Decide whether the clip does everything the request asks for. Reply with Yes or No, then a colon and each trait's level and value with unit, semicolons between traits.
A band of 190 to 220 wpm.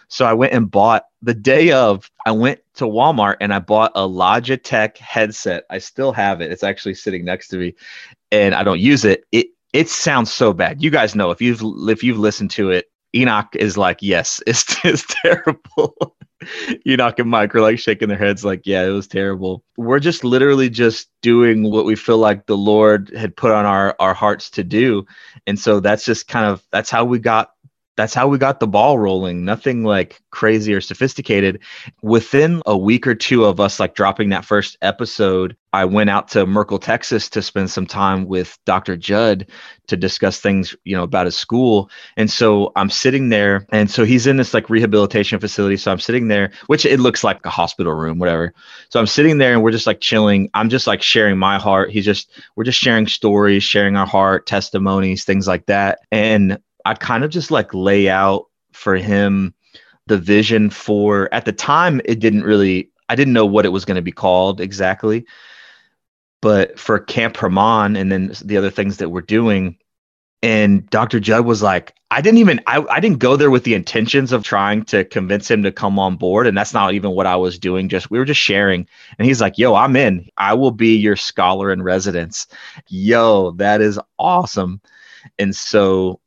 Yes: fast, 205 wpm